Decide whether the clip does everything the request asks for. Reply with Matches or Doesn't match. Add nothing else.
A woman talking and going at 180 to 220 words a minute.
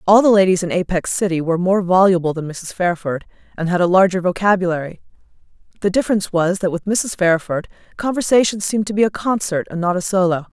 Matches